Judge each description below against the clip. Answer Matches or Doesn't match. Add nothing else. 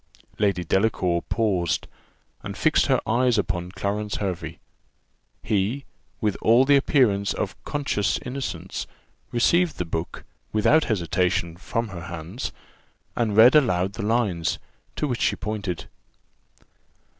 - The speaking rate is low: Matches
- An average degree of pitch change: Matches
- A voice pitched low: Matches